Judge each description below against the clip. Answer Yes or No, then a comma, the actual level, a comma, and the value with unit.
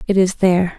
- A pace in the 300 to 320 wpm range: No, fast, 230 wpm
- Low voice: No, medium, 185 Hz